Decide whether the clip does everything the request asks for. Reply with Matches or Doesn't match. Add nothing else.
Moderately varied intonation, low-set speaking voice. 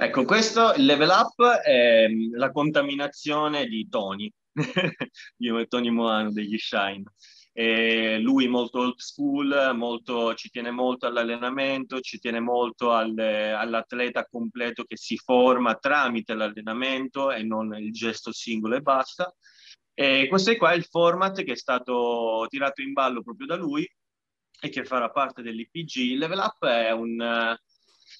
Matches